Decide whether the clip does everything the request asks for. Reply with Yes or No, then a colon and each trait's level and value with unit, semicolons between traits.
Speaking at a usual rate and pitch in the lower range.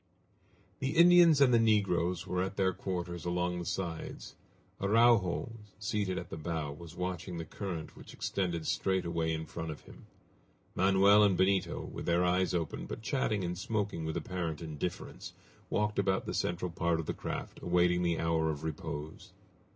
Yes: average, 170 wpm; very low, 90 Hz